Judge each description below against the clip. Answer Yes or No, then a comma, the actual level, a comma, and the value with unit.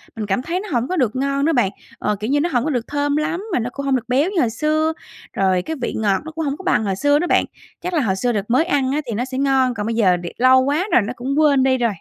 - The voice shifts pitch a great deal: No, average, 4.6 semitones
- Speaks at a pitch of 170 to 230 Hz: No, very high, 260 Hz